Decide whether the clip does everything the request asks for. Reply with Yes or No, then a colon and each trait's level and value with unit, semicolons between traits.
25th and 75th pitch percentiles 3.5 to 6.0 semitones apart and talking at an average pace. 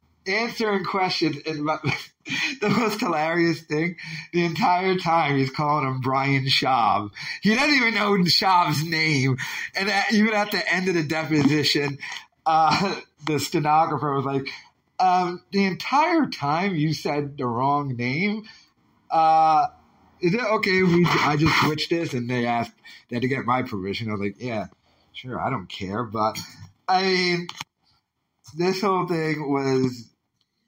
Yes: average, 5.3 semitones; average, 155 wpm